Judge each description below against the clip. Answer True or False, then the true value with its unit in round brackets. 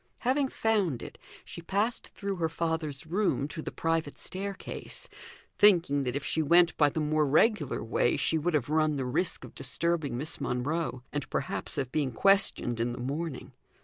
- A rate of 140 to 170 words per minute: False (180 wpm)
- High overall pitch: False (155 Hz)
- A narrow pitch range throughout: False (4.2 semitones)